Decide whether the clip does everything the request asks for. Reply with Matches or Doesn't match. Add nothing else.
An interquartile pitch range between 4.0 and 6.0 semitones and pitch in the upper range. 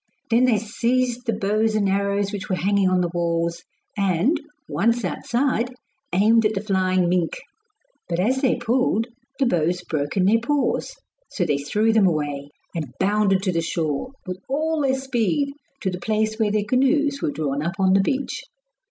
Matches